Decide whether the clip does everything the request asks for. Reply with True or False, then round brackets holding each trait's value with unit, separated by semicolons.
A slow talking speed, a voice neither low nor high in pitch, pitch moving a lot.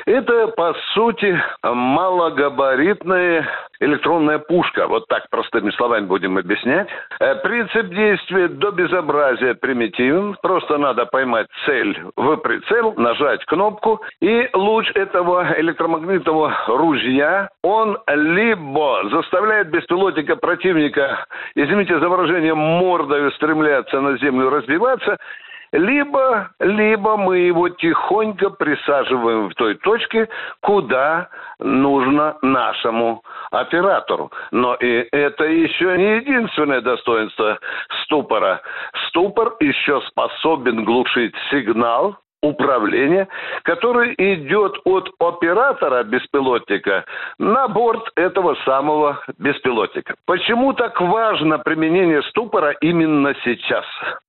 True (95 wpm; 175 Hz; 6.5 semitones)